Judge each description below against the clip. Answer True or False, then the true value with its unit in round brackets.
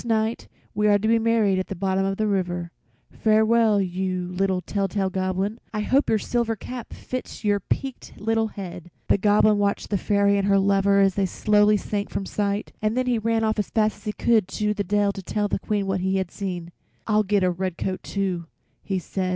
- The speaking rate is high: True (225 wpm)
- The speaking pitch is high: True (200 Hz)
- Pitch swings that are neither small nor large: False (2.1 semitones)